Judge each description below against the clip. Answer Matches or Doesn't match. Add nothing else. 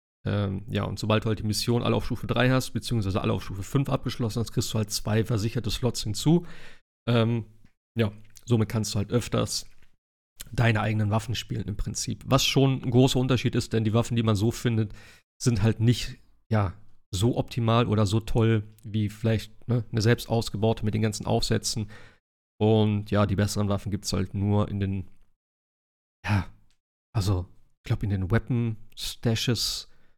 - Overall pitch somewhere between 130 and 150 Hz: Doesn't match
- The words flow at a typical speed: Matches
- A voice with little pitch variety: Matches